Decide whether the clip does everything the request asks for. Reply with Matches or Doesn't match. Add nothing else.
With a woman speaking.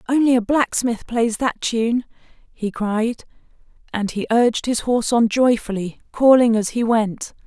Matches